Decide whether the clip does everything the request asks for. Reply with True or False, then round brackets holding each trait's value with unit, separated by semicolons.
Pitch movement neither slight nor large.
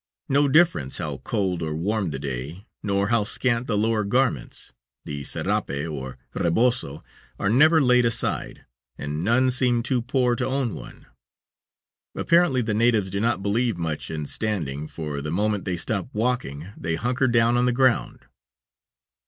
False (7.1 semitones)